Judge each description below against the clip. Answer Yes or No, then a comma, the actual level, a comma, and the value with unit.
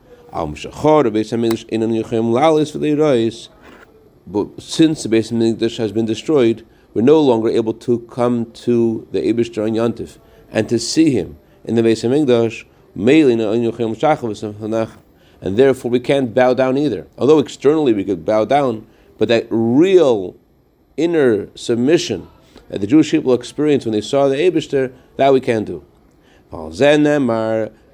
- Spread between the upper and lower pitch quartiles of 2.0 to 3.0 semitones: No, average, 3.7 semitones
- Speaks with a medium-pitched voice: No, low, 115 Hz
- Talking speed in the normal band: No, slow, 120 wpm